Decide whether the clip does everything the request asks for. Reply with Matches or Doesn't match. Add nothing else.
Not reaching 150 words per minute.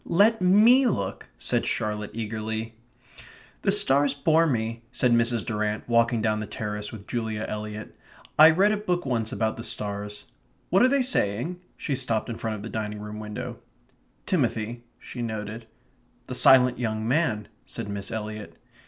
Doesn't match